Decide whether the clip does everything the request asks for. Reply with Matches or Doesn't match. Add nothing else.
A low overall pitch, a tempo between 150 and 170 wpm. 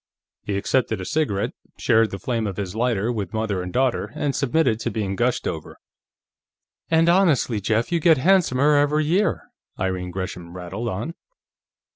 Matches